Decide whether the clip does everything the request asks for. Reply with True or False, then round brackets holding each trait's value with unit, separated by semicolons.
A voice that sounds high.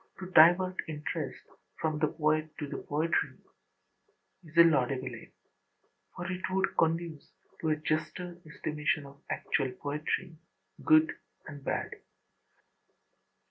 False (155 Hz)